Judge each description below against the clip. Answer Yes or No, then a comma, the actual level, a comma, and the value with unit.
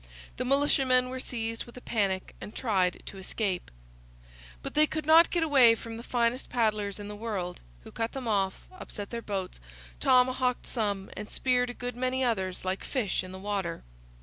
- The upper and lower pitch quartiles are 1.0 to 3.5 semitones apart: No, average, 4.0 semitones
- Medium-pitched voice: No, high, 230 Hz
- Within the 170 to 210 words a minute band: Yes, average, 185 wpm